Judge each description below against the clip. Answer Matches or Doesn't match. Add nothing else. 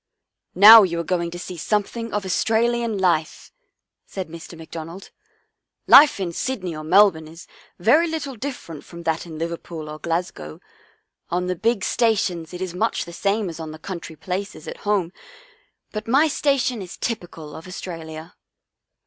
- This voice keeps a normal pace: Matches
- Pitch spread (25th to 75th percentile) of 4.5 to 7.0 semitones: Matches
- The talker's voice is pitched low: Doesn't match